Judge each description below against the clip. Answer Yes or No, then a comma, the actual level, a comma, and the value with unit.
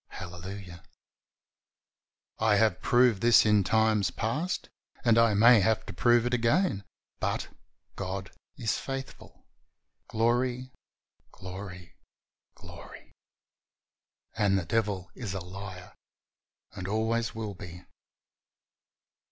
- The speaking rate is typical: No, slow, 105 wpm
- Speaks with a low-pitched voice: Yes, low, 110 Hz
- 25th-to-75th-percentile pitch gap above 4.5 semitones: No, average, 3.5 semitones